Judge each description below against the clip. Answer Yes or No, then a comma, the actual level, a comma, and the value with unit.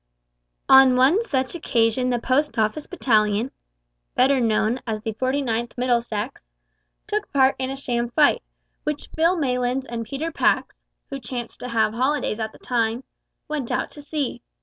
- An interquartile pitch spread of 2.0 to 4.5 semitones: Yes, average, 3.1 semitones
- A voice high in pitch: Yes, very high, 255 Hz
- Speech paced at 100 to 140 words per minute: No, average, 155 wpm